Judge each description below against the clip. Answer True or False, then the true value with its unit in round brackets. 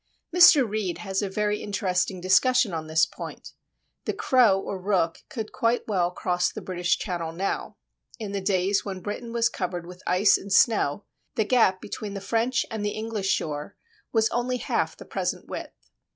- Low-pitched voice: False (200 Hz)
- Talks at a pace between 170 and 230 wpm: True (180 wpm)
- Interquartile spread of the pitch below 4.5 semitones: True (3.5 semitones)